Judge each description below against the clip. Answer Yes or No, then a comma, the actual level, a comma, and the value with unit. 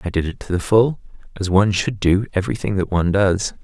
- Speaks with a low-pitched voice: Yes, low, 100 Hz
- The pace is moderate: No, fast, 230 wpm